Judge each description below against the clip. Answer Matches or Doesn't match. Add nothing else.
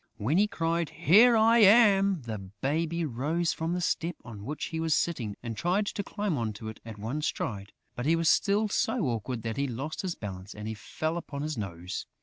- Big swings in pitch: Matches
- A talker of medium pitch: Matches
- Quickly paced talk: Matches